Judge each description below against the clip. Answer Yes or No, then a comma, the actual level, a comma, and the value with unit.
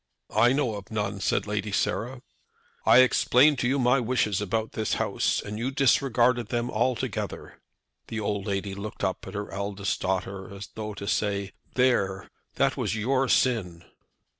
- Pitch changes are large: No, average, 3.7 semitones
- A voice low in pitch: Yes, low, 110 Hz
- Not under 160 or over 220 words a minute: Yes, average, 165 wpm